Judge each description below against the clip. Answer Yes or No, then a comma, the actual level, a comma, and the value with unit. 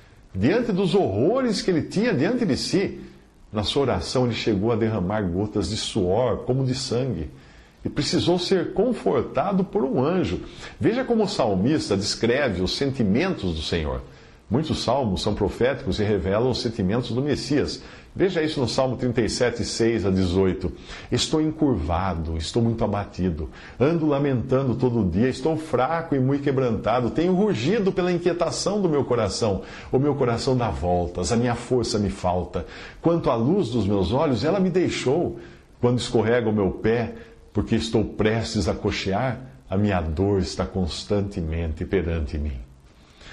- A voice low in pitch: Yes, low, 115 Hz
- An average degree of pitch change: No, wide, 5.9 semitones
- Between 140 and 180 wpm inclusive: Yes, average, 155 wpm